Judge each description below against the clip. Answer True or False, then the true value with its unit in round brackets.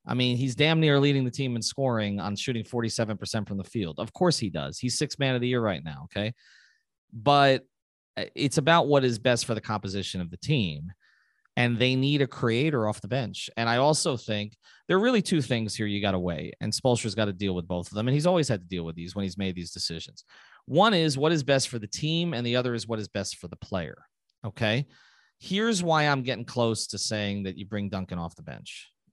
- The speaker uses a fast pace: True (245 wpm)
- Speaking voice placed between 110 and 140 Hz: True (115 Hz)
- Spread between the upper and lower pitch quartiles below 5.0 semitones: False (5.4 semitones)